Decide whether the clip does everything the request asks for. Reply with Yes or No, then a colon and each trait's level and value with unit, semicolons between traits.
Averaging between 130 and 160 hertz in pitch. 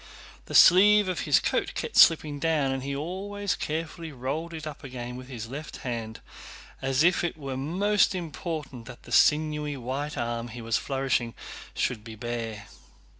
Yes: medium, 140 Hz